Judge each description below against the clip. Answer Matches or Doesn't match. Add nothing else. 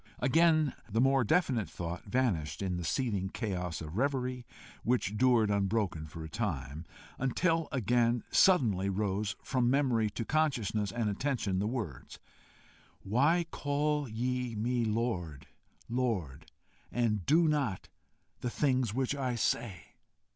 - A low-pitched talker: Matches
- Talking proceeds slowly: Matches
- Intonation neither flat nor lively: Matches